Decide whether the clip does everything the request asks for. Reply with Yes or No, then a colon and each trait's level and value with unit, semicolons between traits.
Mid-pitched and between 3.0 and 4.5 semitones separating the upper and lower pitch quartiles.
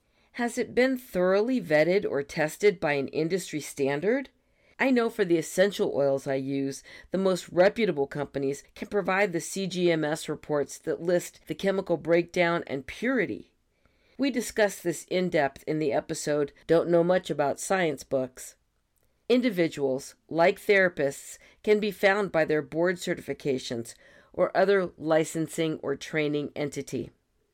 No: medium, 165 Hz; average, 5.2 semitones